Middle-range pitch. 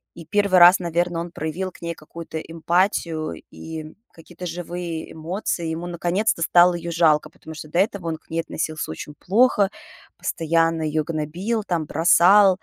Yes: medium, 170 Hz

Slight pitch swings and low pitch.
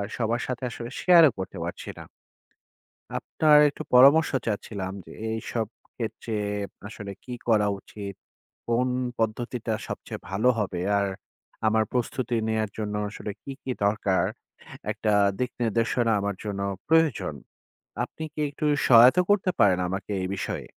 No: average, 3.6 semitones; low, 115 Hz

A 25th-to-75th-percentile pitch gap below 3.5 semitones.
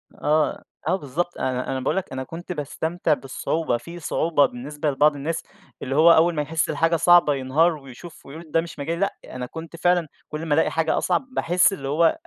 Yes: average, 3.1 semitones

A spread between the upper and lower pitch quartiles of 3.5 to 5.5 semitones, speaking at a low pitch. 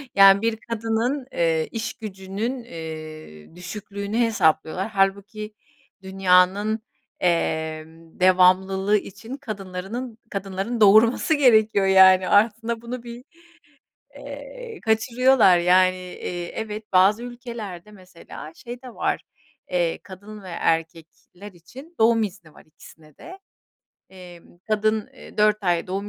No: average, 3.8 semitones; high, 200 Hz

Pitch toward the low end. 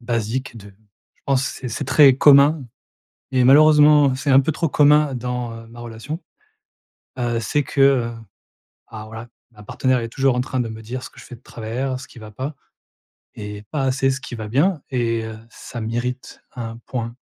Yes: low, 125 Hz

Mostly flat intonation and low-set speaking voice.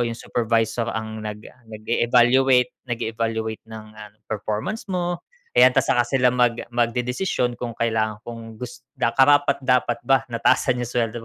Yes: narrow, 2.1 semitones; low, 120 Hz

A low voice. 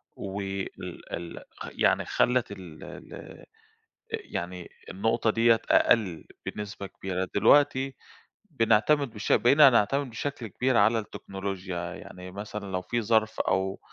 Yes: low, 105 Hz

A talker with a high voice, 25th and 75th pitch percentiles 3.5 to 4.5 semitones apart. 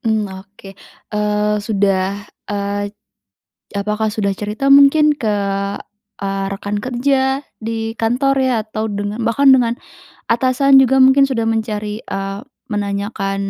Yes: high, 215 Hz; average, 4.0 semitones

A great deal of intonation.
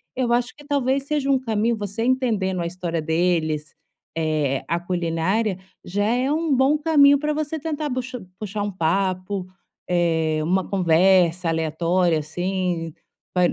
Yes: wide, 7.2 semitones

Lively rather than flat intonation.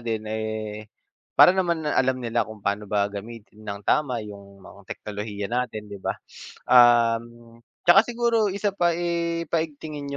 Yes: wide, 7.5 semitones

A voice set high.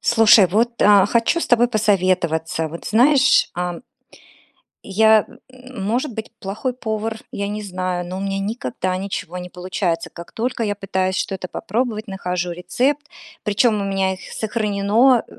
Yes: high, 200 Hz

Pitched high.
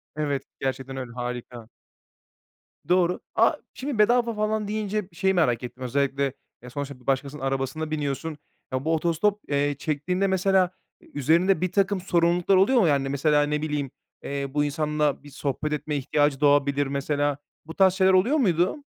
No: medium, 150 Hz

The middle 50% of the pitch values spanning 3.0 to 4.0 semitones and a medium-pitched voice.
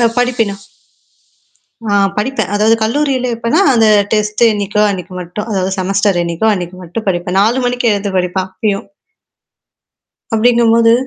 No: average, 3.6 semitones; high, 210 Hz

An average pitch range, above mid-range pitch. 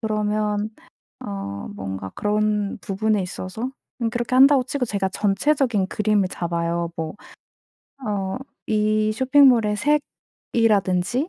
Yes: average, 3.8 semitones; high, 210 Hz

